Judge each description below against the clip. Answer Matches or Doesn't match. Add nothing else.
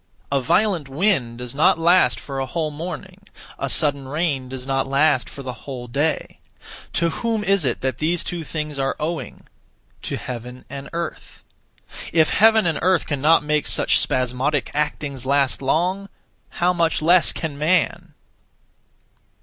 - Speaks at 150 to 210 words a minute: Matches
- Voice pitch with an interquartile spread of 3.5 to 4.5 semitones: Matches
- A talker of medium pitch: Matches